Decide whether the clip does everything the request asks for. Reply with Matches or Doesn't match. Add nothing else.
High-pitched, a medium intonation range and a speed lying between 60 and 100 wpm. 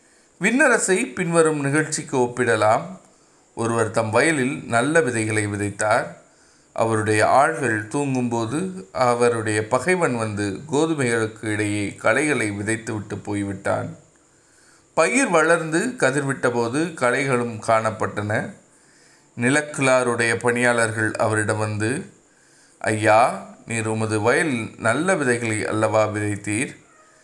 Doesn't match